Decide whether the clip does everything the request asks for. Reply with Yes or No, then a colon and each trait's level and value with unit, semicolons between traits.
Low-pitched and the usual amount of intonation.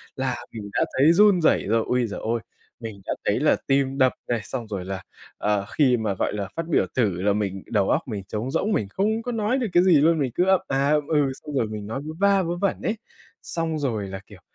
No: low, 130 Hz; wide, 7.8 semitones